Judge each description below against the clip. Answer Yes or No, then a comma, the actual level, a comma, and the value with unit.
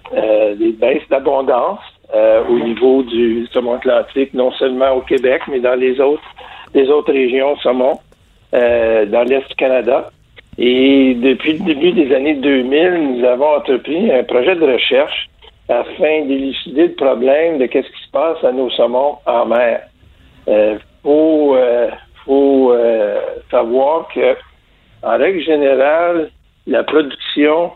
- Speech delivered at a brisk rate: No, slow, 145 wpm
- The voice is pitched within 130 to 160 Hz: Yes, low, 135 Hz